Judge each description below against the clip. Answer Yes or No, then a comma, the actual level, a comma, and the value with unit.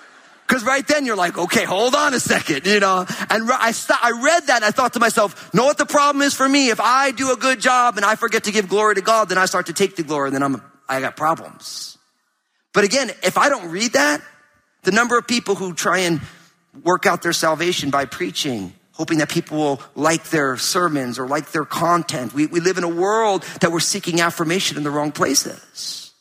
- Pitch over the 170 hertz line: Yes, medium, 185 Hz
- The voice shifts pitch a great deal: Yes, wide, 6.3 semitones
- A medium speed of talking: No, fast, 235 wpm